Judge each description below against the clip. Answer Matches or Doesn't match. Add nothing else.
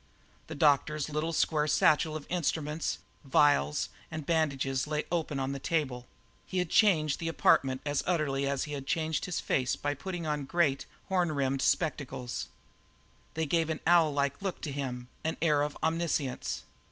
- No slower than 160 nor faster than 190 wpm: Matches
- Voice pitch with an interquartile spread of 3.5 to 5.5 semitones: Doesn't match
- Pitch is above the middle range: Doesn't match